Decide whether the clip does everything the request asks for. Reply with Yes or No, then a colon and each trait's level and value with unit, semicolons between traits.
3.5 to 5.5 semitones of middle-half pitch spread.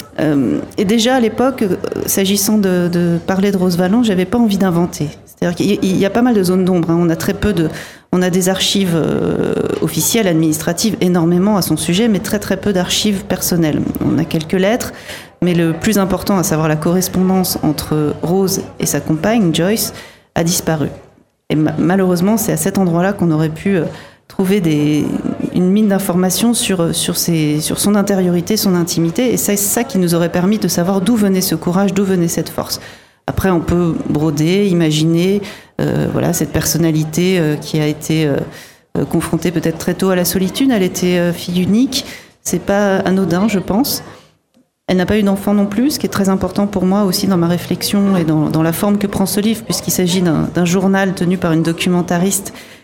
No: average, 3.1 semitones